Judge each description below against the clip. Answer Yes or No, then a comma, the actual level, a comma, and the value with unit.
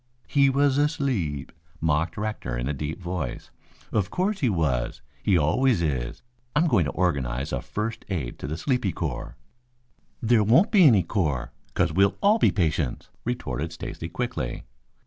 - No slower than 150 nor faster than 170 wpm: Yes, average, 160 wpm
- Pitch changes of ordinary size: No, wide, 8.9 semitones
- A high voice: No, very low, 90 Hz